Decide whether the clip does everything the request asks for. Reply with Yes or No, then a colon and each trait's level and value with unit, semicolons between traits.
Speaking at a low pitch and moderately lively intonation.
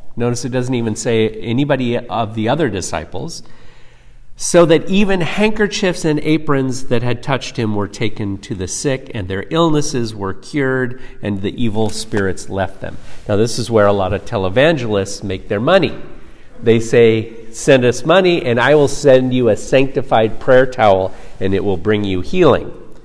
Yes: low, 120 Hz; average, 4.7 semitones